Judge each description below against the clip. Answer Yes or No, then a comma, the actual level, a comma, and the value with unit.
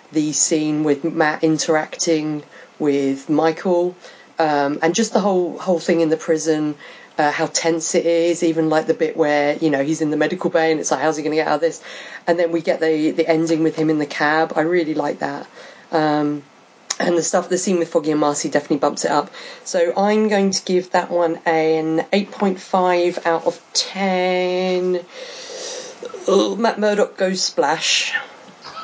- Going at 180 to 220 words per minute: Yes, average, 190 wpm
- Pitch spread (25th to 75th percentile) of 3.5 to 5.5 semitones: No, narrow, 2.6 semitones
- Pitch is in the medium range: Yes, medium, 165 Hz